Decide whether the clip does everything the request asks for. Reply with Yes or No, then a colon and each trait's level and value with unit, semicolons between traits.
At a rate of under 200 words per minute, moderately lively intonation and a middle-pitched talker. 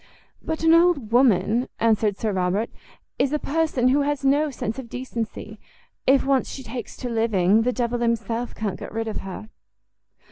No: average, 175 wpm; average, 3.7 semitones; high, 235 Hz